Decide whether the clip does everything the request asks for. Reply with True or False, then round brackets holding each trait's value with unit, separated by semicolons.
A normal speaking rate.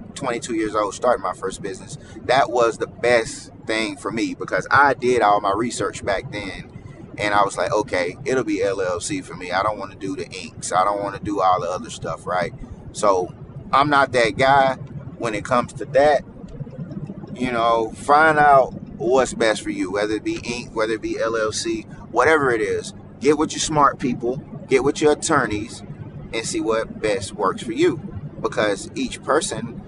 True (195 wpm)